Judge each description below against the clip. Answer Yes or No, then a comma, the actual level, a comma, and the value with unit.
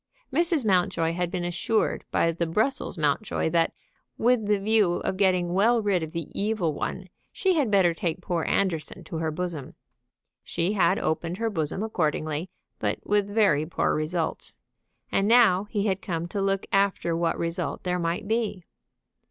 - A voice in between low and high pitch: Yes, medium, 180 Hz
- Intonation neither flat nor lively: Yes, average, 3.7 semitones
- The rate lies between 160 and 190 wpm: Yes, average, 170 wpm